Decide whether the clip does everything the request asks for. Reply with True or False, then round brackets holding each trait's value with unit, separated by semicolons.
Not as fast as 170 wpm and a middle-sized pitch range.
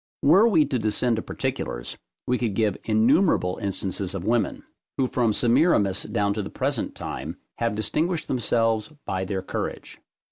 True (155 wpm; 4.6 semitones)